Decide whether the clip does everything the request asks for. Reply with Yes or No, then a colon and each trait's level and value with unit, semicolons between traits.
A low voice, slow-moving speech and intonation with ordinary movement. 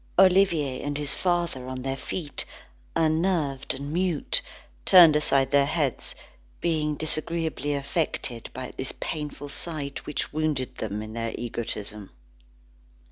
No: medium, 145 Hz; slow, 125 wpm; average, 3.6 semitones